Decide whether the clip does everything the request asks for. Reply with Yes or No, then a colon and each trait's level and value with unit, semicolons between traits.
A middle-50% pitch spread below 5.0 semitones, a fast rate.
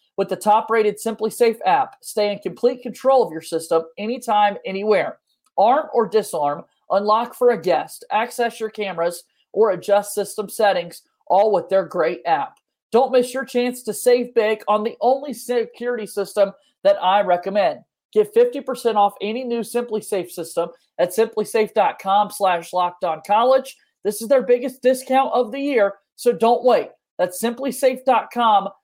No: average, 3.8 semitones; average, 155 wpm